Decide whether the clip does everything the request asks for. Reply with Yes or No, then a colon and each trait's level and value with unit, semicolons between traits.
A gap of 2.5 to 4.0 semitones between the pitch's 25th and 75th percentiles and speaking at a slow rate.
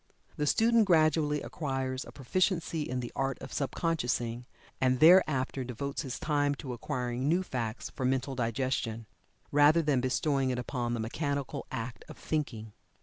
No: average, 3.2 semitones; average, 155 wpm